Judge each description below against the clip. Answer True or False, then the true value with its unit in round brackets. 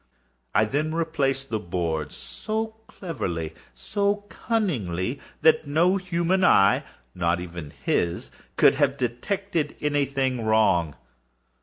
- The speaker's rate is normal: False (105 wpm)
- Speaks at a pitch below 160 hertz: True (135 Hz)